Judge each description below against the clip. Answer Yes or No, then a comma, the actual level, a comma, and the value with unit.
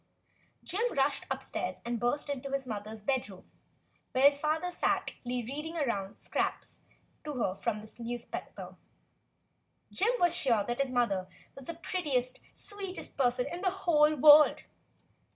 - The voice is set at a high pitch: Yes, very high, 270 Hz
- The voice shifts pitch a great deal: No, average, 4.4 semitones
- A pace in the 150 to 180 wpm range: No, average, 140 wpm